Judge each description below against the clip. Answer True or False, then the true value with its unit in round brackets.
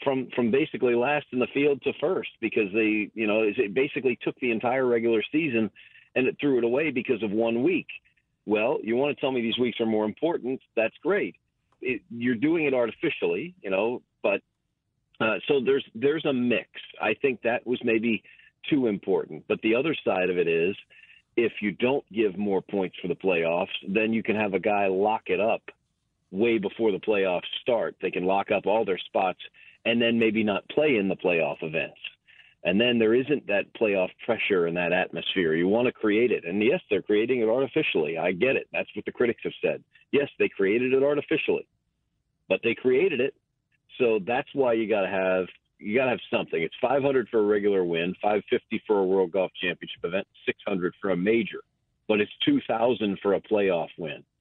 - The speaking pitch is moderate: False (120 Hz)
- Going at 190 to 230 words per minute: True (200 wpm)